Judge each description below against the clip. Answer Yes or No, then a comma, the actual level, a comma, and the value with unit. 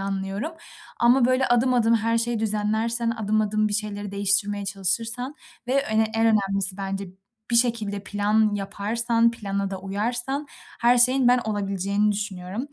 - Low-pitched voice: No, high, 215 Hz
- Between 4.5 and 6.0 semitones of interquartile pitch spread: No, average, 2.8 semitones